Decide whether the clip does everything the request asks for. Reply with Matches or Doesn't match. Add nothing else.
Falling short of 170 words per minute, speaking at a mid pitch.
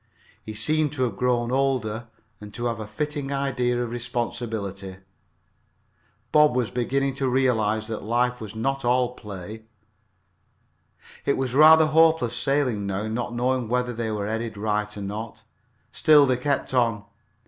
Doesn't match